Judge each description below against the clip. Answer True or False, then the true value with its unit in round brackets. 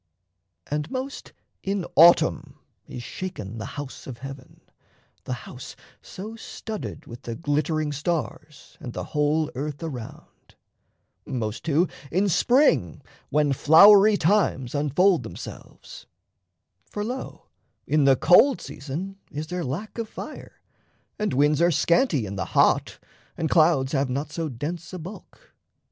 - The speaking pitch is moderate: True (155 Hz)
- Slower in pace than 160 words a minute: True (135 wpm)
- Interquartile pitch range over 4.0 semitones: True (5.2 semitones)